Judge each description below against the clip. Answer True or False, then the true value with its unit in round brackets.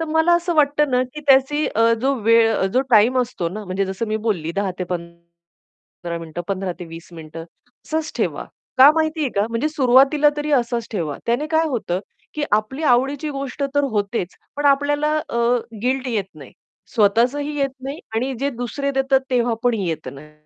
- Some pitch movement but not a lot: False (6.5 semitones)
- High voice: True (245 Hz)